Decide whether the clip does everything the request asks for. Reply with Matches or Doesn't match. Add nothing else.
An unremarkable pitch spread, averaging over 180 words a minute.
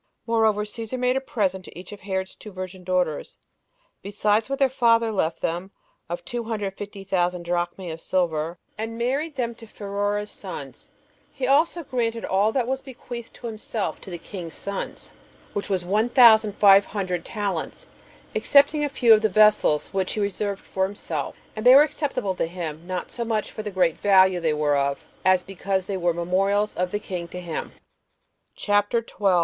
Matches